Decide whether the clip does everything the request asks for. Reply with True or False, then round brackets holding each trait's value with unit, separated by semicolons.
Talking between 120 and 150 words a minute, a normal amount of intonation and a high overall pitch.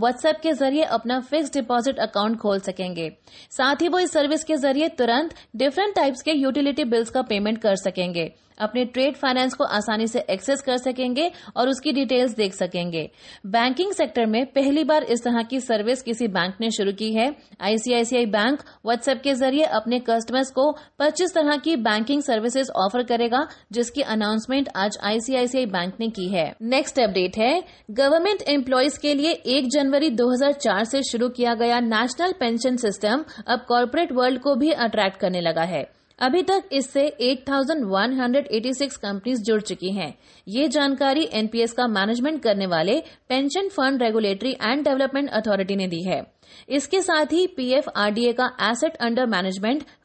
False (165 wpm; 4.3 semitones; 250 Hz)